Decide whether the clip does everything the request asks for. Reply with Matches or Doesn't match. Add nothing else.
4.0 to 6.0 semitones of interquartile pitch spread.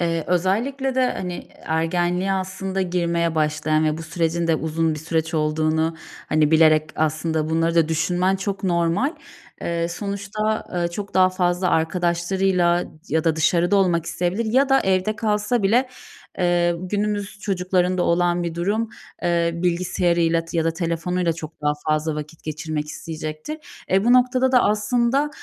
Doesn't match